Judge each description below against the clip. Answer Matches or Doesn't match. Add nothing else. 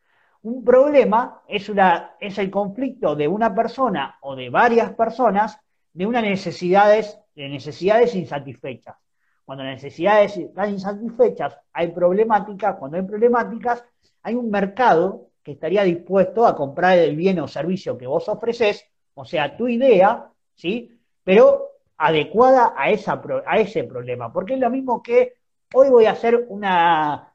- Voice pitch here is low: Doesn't match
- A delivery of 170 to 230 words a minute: Doesn't match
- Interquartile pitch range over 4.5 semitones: Matches